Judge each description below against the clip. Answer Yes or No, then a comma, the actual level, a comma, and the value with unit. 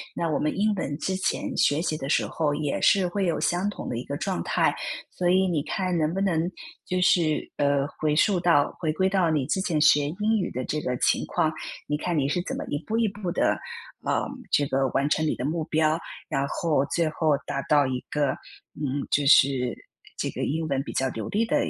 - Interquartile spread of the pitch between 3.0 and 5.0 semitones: Yes, average, 4.0 semitones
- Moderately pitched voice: Yes, medium, 155 Hz